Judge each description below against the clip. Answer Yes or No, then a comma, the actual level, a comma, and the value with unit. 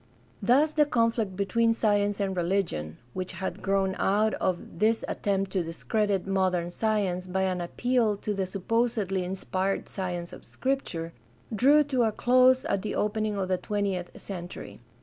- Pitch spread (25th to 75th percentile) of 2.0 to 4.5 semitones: Yes, average, 3.3 semitones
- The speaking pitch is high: Yes, high, 195 Hz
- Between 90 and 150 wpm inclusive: No, average, 160 wpm